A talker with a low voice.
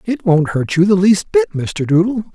No: medium, 175 Hz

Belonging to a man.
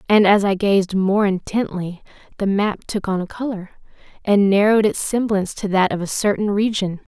No: female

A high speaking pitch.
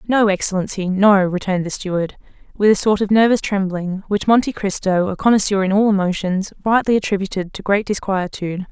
Yes: high, 195 Hz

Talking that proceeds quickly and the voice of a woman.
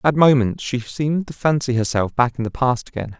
No: fast, 225 wpm; male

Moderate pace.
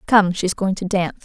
No: fast, 240 wpm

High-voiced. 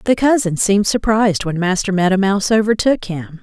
Yes: high, 200 Hz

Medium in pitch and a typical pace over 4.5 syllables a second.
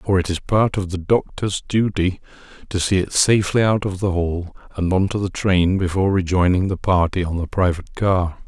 No: very low, 95 Hz; 5.2 syllables/s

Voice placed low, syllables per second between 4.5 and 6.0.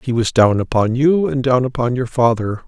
Yes: low, 125 Hz; 5.1 syllables/s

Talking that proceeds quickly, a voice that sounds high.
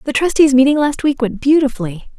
No: average, 190 wpm; very high, 265 Hz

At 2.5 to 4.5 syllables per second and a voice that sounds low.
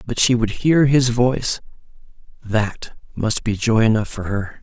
Yes: 4.3 syllables/s; low, 115 Hz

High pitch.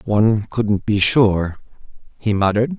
No: low, 105 Hz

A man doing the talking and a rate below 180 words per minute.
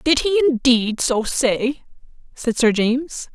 No: female; average, 145 wpm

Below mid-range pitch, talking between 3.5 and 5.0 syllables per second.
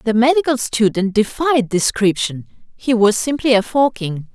No: high, 230 Hz; 4.6 syllables/s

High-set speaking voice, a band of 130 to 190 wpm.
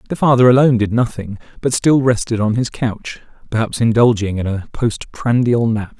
No: low, 115 Hz; average, 170 wpm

